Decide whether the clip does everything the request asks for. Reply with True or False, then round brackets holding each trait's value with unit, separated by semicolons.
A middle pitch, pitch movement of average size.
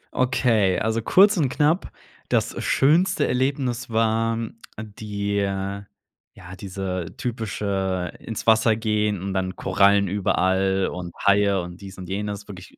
False (100 Hz; 3.0 semitones)